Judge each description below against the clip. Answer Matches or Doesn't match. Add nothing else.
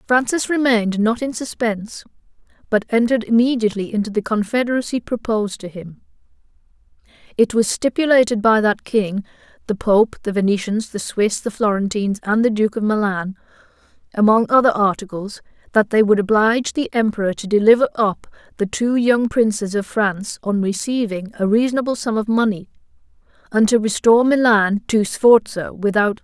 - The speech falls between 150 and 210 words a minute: Matches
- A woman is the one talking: Matches